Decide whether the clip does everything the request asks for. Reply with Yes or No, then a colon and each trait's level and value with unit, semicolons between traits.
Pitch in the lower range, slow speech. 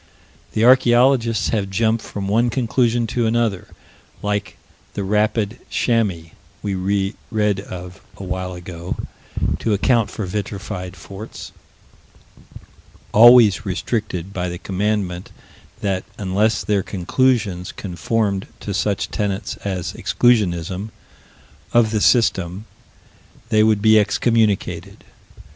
Yes: low, 105 Hz; slow, 110 wpm